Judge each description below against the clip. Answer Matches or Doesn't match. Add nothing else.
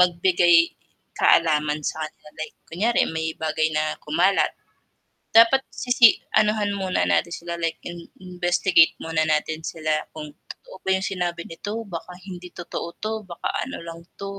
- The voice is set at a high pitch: Doesn't match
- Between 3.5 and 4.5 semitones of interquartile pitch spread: Doesn't match